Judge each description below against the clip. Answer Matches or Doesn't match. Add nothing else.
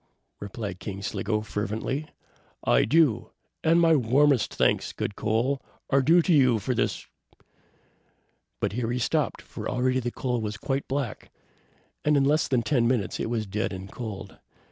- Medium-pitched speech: Doesn't match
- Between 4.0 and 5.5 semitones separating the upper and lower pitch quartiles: Matches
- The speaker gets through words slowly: Doesn't match